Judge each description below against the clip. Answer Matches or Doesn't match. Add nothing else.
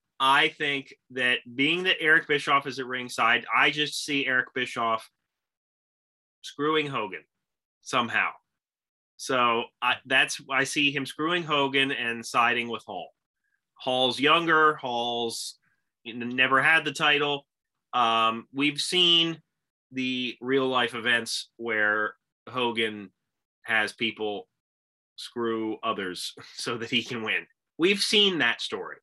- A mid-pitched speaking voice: Doesn't match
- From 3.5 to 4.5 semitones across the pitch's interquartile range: Matches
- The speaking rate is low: Matches